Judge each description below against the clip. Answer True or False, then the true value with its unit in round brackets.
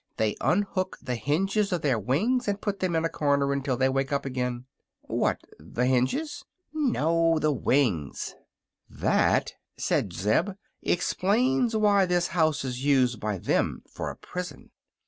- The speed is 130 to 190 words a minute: True (150 wpm)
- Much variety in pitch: True (7.1 semitones)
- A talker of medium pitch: True (150 Hz)